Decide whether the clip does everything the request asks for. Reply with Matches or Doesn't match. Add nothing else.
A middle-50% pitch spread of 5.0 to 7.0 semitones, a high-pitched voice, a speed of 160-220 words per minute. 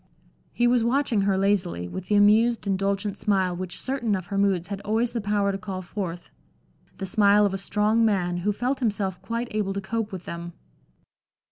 Doesn't match